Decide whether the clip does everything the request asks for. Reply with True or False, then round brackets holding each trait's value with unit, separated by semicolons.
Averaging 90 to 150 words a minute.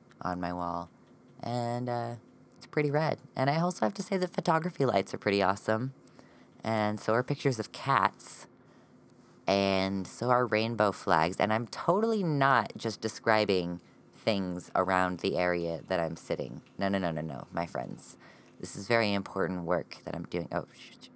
False (175 wpm)